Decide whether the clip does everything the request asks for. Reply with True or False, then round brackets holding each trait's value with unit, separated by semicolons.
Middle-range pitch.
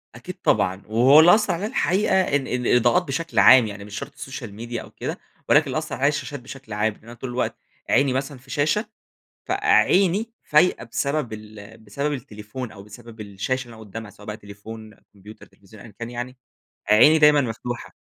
False (120 Hz)